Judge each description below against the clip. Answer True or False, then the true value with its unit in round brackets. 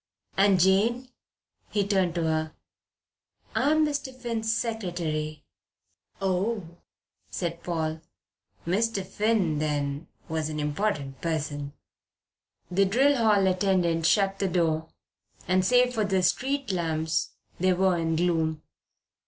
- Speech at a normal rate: False (115 wpm)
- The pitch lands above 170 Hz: True (185 Hz)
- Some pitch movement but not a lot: True (4.9 semitones)